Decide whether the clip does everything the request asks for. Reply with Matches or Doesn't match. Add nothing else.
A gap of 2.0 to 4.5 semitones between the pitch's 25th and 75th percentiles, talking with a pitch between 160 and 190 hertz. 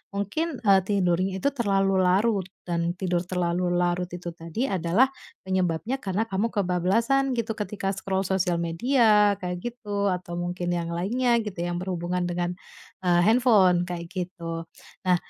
Matches